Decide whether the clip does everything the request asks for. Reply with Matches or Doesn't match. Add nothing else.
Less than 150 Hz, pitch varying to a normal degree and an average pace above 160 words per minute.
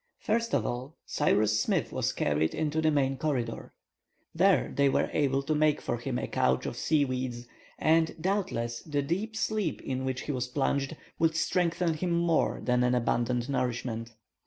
Matches